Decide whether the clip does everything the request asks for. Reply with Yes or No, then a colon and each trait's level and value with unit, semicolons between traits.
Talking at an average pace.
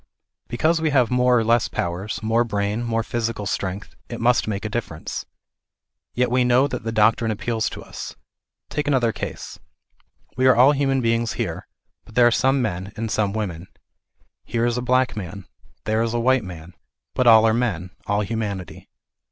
Yes: average, 180 wpm